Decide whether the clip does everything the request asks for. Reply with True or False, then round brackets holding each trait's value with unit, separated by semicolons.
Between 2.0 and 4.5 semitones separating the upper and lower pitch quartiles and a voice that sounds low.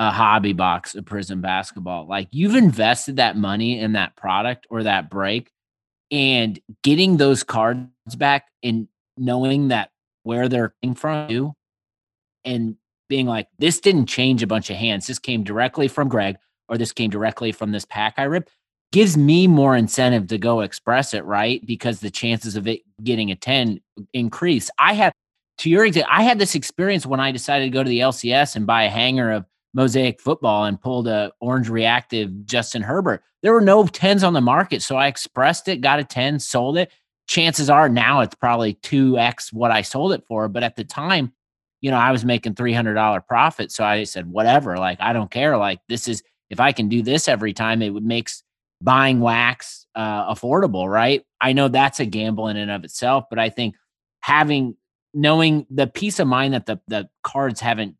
True (4.0 semitones; 120 Hz)